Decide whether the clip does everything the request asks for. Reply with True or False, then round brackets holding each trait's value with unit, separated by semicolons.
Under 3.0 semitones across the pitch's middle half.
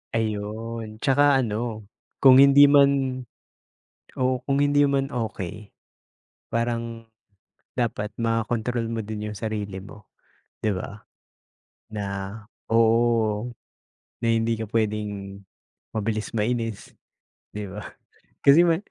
True (2.6 semitones)